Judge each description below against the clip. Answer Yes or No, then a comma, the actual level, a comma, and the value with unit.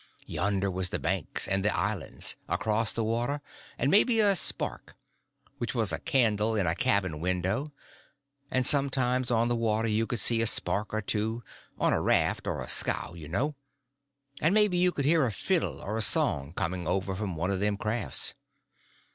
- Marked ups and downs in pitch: No, average, 4.6 semitones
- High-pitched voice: No, low, 110 Hz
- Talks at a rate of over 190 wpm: No, average, 180 wpm